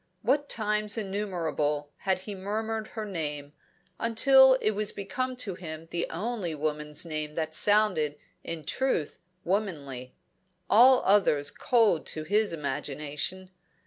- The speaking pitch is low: No, high, 190 Hz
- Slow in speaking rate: Yes, slow, 125 wpm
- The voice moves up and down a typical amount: No, wide, 5.9 semitones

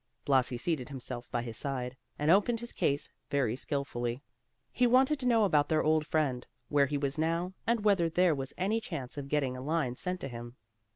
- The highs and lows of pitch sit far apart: Yes, wide, 5.9 semitones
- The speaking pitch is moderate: Yes, medium, 145 Hz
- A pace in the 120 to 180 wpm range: No, fast, 205 wpm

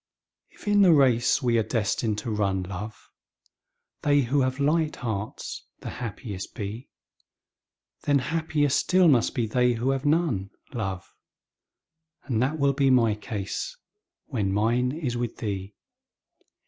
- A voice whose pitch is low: Yes, low, 120 Hz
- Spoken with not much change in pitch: No, average, 5.0 semitones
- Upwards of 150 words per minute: No, average, 140 wpm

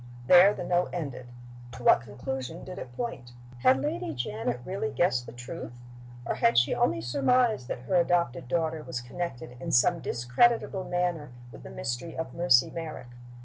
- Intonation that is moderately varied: No, wide, 6.2 semitones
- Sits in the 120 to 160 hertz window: Yes, medium, 140 Hz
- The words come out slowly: No, average, 170 wpm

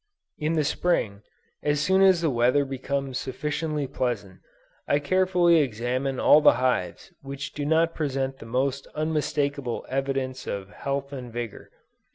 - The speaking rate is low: No, average, 145 wpm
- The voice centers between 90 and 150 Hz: Yes, medium, 140 Hz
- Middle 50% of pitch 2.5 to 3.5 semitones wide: Yes, average, 3.0 semitones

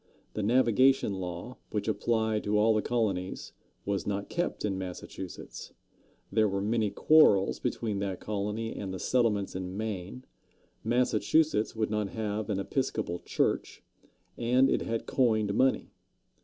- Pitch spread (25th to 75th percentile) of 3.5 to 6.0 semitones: No, average, 2.9 semitones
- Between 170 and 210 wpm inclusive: No, average, 140 wpm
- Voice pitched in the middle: No, low, 105 Hz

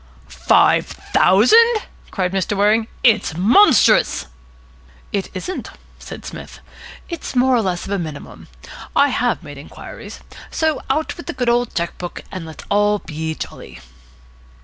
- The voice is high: Yes, high, 205 Hz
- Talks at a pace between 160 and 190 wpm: No, average, 145 wpm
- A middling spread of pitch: No, wide, 6.1 semitones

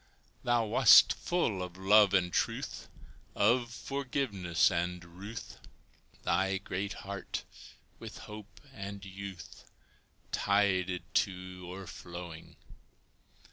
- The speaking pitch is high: No, very low, 95 Hz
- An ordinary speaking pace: No, slow, 95 wpm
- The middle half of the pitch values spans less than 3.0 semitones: Yes, narrow, 2.6 semitones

